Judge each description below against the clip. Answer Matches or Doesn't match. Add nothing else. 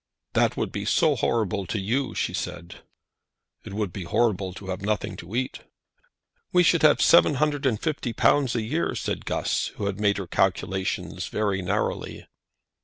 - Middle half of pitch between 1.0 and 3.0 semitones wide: Doesn't match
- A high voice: Doesn't match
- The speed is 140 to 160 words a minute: Doesn't match